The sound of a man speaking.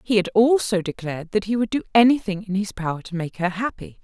No: female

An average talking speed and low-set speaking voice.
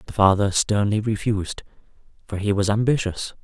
Yes: average, 155 wpm; low, 105 Hz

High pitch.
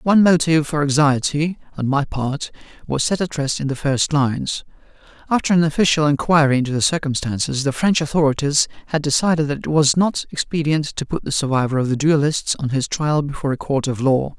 No: medium, 145 Hz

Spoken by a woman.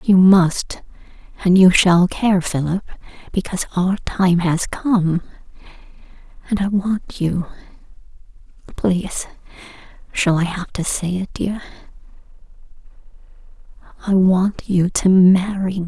Yes: female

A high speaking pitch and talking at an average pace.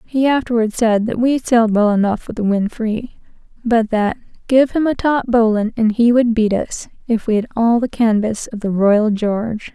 No: high, 225 Hz; fast, 210 wpm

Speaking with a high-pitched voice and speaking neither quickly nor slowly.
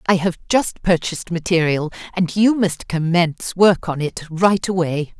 No: medium, 175 Hz; average, 160 wpm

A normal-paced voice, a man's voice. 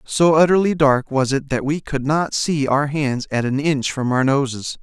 No: fast, 225 wpm; male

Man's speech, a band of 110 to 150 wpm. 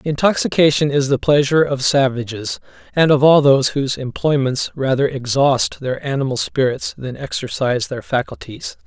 Yes: male; average, 140 wpm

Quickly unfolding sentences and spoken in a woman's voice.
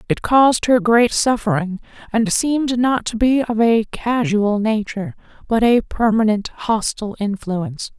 No: average, 145 wpm; female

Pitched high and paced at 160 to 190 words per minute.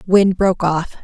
No: medium, 180 Hz; average, 175 wpm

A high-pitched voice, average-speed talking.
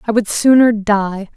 Yes: high, 215 Hz; average, 175 wpm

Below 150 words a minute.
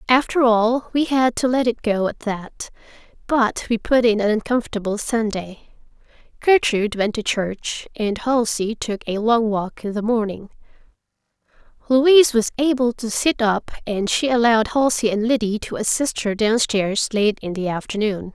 No: average, 165 wpm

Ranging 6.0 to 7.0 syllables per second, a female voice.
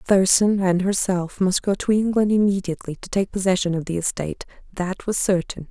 No: 5.4 syllables/s; female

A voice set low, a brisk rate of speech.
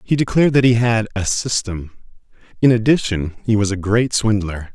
No: low, 110 Hz; average, 175 wpm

